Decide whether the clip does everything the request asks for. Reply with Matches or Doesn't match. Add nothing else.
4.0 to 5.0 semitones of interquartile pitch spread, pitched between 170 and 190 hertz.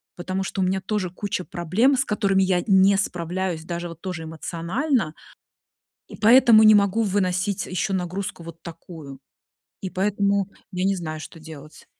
Doesn't match